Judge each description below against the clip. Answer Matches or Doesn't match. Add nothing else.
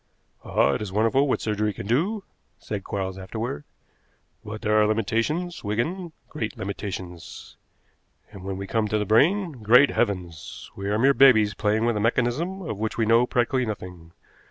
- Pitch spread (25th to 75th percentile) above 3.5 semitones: Matches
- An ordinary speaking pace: Matches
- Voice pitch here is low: Matches